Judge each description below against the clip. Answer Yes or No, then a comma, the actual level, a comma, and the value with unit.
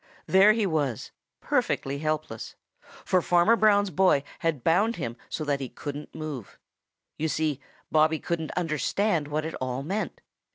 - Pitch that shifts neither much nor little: Yes, average, 4.2 semitones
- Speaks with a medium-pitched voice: Yes, medium, 155 Hz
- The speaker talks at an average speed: Yes, average, 150 wpm